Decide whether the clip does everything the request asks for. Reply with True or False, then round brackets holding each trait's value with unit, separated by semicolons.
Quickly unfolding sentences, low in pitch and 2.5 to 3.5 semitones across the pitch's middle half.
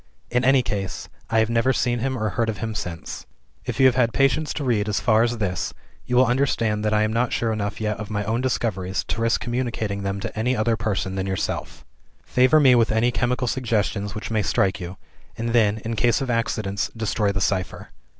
True (220 wpm; 110 Hz; 3.0 semitones)